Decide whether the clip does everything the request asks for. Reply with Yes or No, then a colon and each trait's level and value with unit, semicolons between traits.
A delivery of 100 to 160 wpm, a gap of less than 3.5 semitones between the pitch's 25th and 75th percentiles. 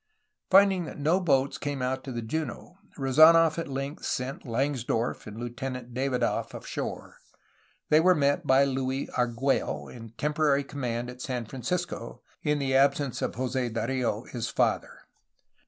Yes: average, 150 wpm; average, 2.8 semitones